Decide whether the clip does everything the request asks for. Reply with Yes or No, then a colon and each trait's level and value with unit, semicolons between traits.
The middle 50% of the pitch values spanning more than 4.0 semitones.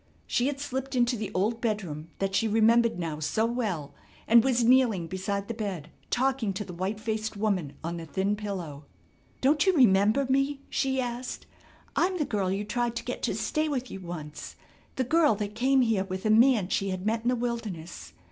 Yes: average, 4.7 semitones